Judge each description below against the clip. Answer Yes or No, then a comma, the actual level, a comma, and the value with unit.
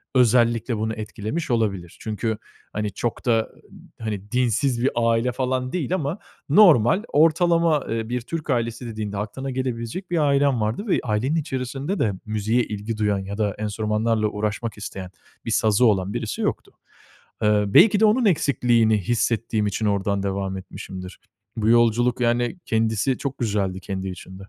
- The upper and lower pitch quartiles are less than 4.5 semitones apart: Yes, average, 3.5 semitones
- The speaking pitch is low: Yes, low, 115 Hz